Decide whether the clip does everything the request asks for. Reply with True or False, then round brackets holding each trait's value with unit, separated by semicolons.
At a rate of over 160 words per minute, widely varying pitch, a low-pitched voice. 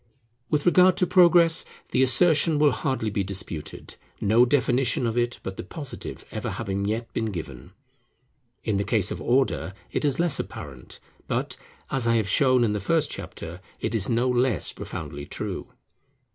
True (170 wpm; 6.4 semitones; 120 Hz)